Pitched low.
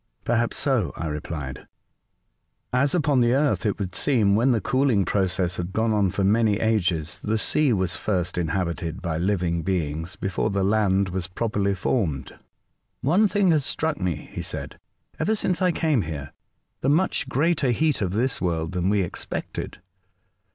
Yes: low, 100 Hz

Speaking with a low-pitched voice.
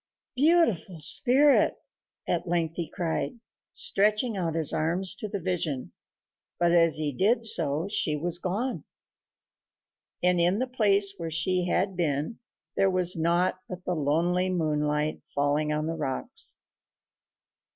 No: medium, 175 Hz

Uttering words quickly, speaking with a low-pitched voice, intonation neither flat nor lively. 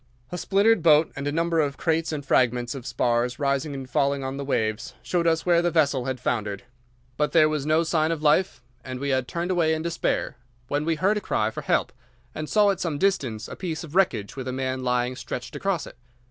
No: fast, 230 wpm; medium, 150 Hz; average, 4.4 semitones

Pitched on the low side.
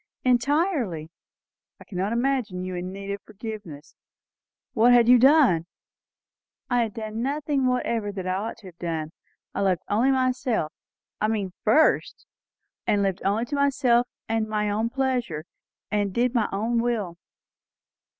No: high, 220 Hz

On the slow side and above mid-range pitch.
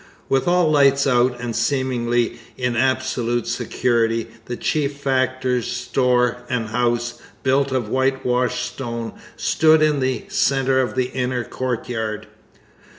No: slow, 125 wpm; low, 125 Hz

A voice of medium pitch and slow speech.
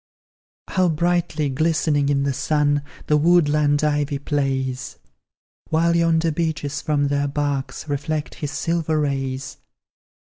Yes: medium, 150 Hz; slow, 115 wpm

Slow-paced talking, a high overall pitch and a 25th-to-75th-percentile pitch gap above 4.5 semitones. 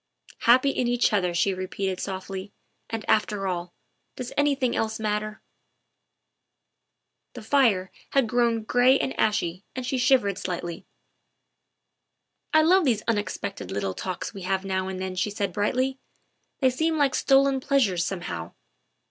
No: average, 165 wpm; high, 215 Hz; wide, 5.4 semitones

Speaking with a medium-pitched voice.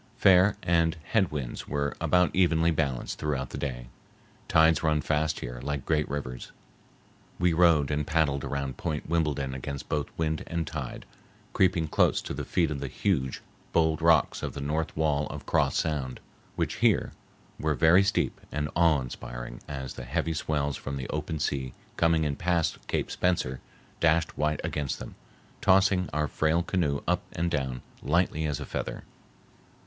No: very low, 75 Hz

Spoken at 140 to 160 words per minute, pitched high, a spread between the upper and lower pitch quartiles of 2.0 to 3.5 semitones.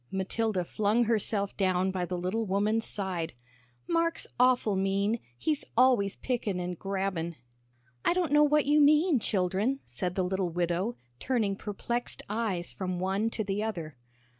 No: average, 150 wpm; high, 200 Hz; average, 4.3 semitones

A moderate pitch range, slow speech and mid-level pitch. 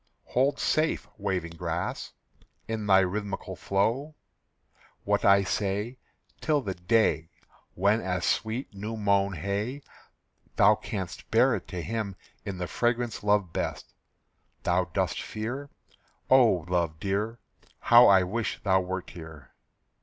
No: average, 3.6 semitones; slow, 130 wpm; low, 100 Hz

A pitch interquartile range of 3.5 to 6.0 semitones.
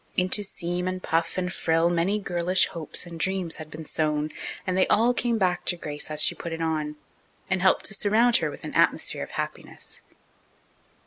No: average, 2.7 semitones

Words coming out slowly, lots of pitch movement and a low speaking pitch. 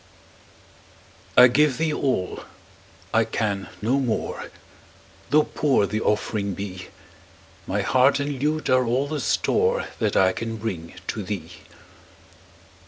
Yes: slow, 125 wpm; wide, 5.8 semitones; low, 115 Hz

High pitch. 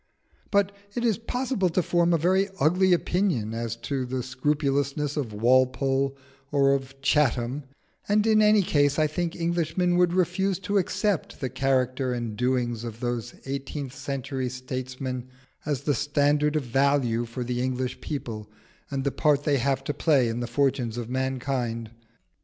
No: low, 135 Hz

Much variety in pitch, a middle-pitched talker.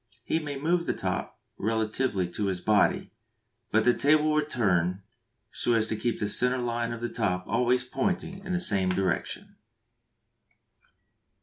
No: wide, 5.8 semitones; low, 115 Hz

